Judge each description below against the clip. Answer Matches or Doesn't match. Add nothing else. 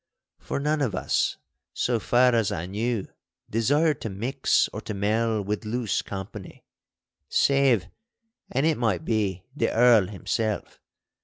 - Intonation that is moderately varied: Matches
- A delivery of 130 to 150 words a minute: Matches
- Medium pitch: Doesn't match